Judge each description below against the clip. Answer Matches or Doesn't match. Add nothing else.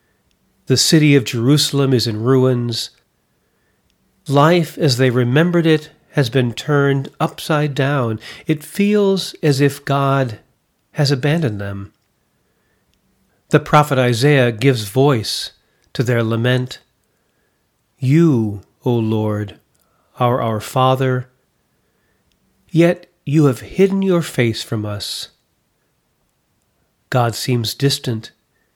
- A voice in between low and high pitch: Doesn't match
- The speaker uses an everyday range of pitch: Matches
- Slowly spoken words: Matches